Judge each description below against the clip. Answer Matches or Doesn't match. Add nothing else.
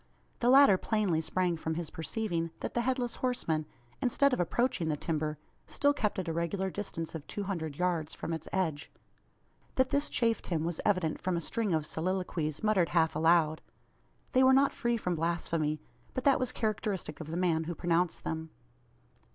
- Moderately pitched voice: Matches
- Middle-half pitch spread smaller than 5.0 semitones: Doesn't match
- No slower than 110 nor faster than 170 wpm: Doesn't match